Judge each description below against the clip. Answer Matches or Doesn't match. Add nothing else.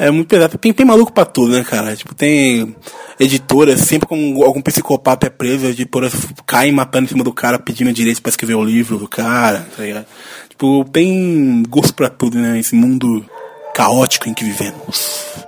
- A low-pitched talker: Matches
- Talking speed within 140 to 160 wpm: Doesn't match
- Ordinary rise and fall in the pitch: Matches